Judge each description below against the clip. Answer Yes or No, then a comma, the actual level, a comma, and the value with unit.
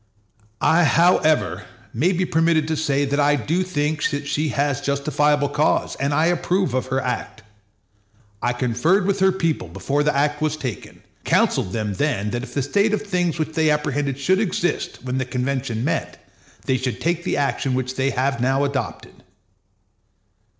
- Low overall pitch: No, medium, 145 Hz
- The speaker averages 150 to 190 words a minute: Yes, average, 175 wpm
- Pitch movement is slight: No, average, 3.7 semitones